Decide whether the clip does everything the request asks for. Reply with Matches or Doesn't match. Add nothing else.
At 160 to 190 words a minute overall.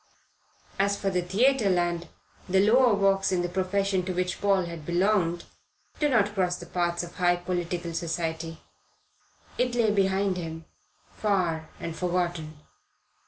Doesn't match